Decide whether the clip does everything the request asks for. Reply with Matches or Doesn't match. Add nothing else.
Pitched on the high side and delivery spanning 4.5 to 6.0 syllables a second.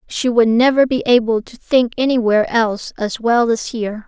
Matches